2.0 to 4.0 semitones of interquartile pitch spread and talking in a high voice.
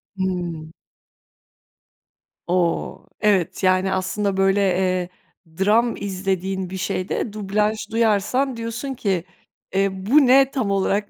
Yes: average, 2.7 semitones; high, 195 Hz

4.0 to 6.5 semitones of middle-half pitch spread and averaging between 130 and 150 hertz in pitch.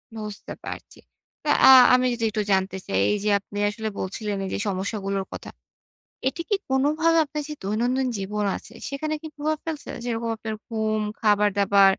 No: average, 4.7 semitones; high, 215 Hz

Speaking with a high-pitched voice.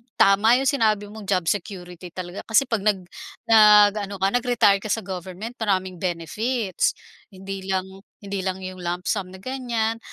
Yes: high, 200 Hz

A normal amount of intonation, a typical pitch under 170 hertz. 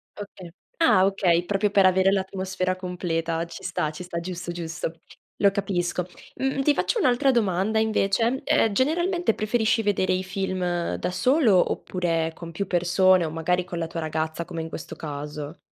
No: average, 3.4 semitones; medium, 185 Hz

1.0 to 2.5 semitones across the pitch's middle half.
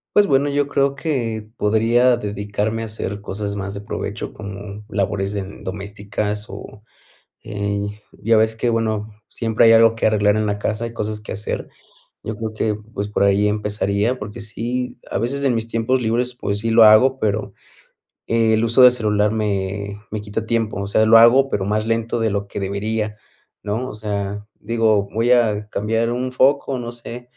Yes: narrow, 2.1 semitones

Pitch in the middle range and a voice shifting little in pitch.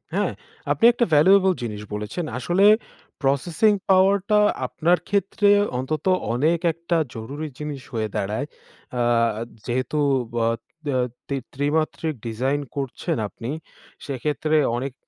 No: medium, 150 Hz; average, 5.3 semitones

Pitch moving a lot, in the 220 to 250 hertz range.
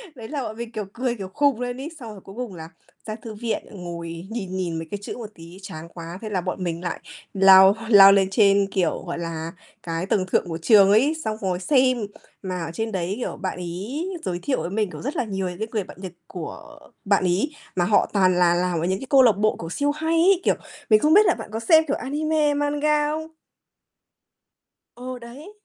No: wide, 5.9 semitones; high, 205 Hz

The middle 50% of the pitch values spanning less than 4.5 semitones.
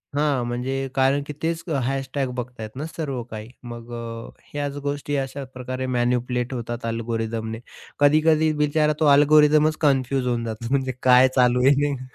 Yes: average, 3.1 semitones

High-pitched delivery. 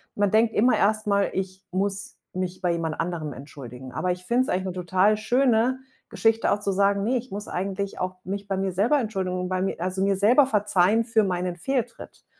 Yes: high, 195 Hz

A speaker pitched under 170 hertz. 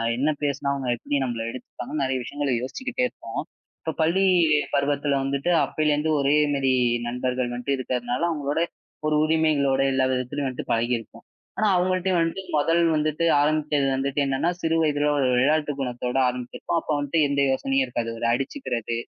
Yes: medium, 140 Hz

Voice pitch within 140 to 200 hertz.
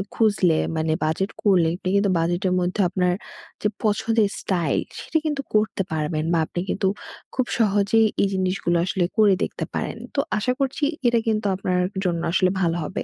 Yes: high, 190 Hz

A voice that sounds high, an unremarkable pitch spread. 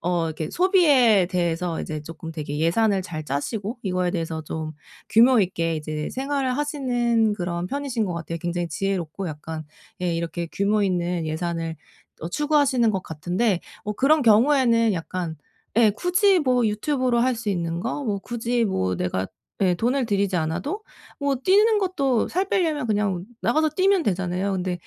No: high, 200 Hz; wide, 7.1 semitones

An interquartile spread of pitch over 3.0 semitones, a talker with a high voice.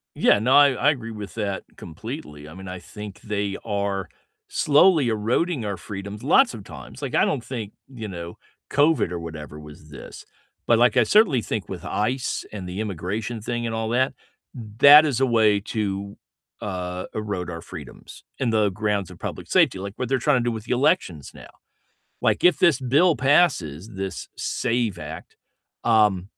No: average, 4.6 semitones; low, 110 Hz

